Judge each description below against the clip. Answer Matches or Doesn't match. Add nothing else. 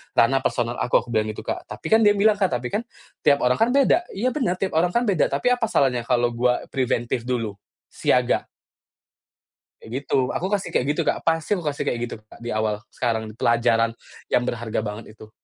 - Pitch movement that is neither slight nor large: Doesn't match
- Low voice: Matches